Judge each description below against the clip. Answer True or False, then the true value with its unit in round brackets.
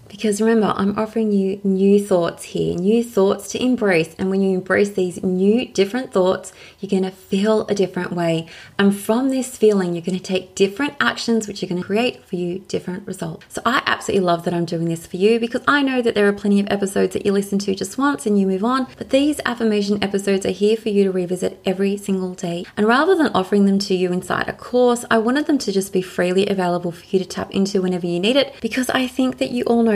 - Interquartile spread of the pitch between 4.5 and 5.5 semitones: False (3.3 semitones)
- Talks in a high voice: True (200 Hz)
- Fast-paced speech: True (245 wpm)